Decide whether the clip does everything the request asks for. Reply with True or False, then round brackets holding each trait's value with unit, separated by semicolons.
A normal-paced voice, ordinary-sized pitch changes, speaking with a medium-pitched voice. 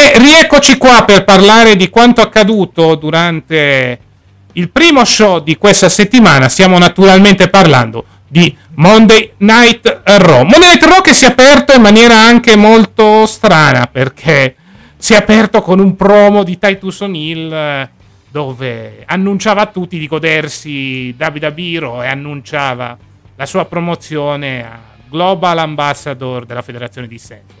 False (140 wpm; 7.8 semitones; 175 Hz)